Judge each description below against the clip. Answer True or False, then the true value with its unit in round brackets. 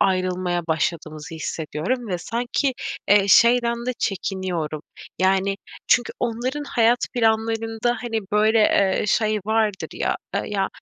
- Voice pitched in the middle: False (210 Hz)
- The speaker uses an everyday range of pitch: True (4.2 semitones)